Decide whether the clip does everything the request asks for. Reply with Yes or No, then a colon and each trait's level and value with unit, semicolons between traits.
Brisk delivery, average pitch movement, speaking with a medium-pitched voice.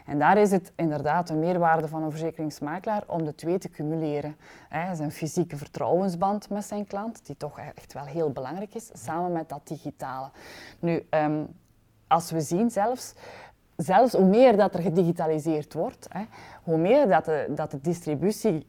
No: average, 175 wpm; average, 4.0 semitones; medium, 165 Hz